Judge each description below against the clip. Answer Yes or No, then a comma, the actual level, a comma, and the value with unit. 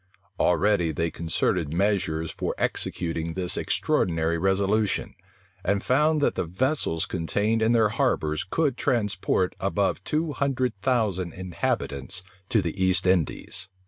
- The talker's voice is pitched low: Yes, very low, 95 Hz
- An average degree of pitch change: Yes, average, 4.9 semitones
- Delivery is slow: Yes, slow, 125 wpm